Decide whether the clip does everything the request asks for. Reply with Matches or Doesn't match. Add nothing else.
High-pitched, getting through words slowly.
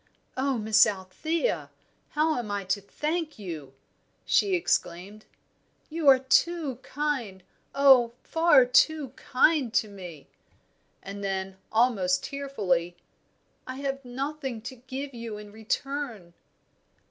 Matches